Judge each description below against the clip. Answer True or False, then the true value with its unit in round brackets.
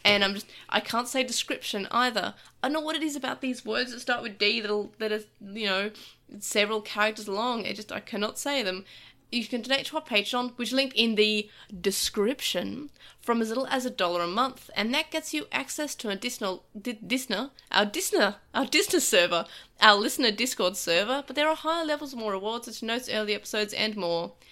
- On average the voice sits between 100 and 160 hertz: False (225 Hz)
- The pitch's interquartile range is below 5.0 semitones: True (4.2 semitones)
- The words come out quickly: True (210 wpm)